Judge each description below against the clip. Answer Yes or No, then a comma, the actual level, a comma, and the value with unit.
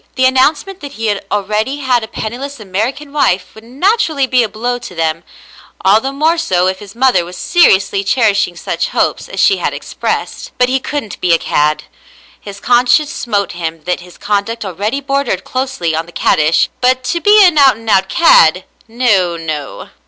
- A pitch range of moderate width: No, wide, 6.1 semitones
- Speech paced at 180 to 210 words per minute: Yes, average, 190 wpm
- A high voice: Yes, high, 225 Hz